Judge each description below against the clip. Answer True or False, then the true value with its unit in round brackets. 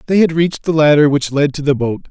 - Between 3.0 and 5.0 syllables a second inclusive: False (6.3 syllables/s)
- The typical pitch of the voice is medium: True (150 Hz)